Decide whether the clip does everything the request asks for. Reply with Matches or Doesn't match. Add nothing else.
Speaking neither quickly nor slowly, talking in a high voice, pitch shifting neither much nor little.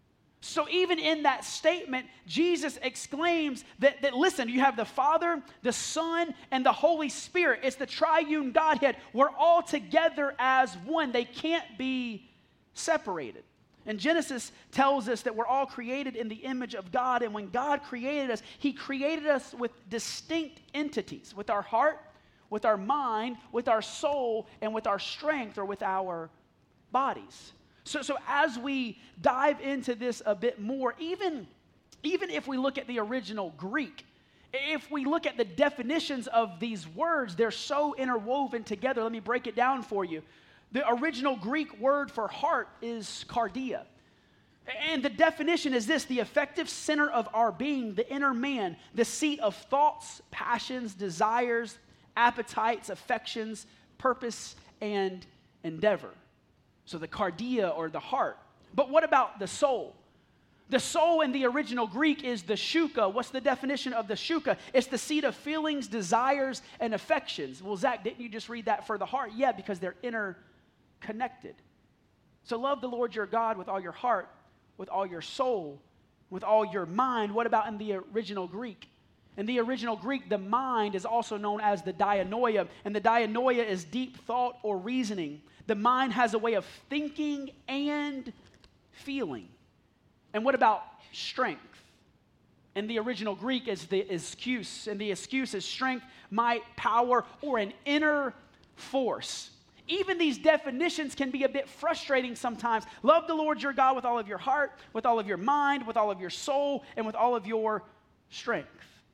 Matches